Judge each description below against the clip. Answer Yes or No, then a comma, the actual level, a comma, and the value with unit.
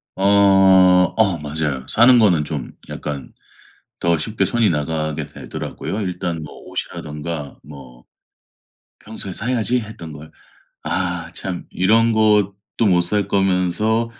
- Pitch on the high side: No, very low, 90 Hz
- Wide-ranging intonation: Yes, wide, 5.8 semitones